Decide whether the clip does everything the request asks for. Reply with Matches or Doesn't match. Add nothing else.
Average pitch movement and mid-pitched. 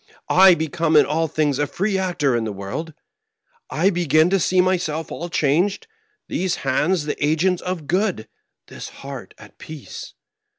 Matches